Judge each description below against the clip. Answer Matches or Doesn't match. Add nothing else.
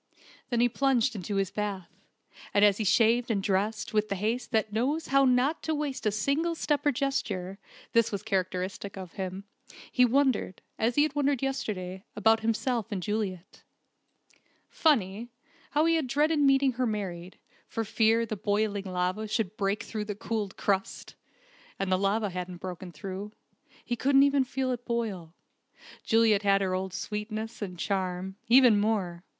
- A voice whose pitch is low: Doesn't match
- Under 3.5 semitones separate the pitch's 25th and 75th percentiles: Doesn't match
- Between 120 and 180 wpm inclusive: Matches